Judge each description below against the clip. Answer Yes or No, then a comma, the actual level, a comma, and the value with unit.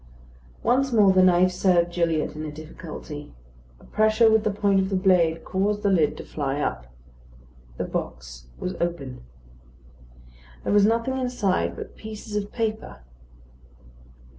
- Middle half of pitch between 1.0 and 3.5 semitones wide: No, average, 5.2 semitones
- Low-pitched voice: No, medium, 185 Hz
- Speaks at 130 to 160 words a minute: Yes, average, 145 wpm